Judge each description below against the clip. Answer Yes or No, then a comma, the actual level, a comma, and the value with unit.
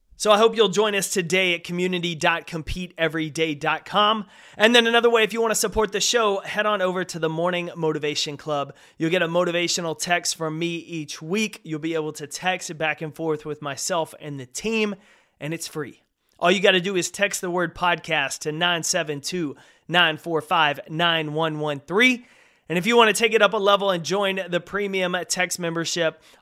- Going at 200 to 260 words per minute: No, average, 190 wpm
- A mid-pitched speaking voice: Yes, medium, 175 Hz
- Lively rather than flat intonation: No, average, 3.8 semitones